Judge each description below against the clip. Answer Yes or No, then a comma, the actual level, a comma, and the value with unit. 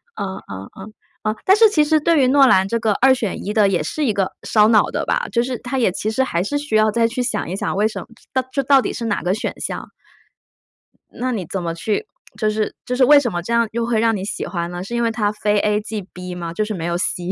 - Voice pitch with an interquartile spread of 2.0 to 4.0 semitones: No, average, 4.5 semitones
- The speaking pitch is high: Yes, high, 215 Hz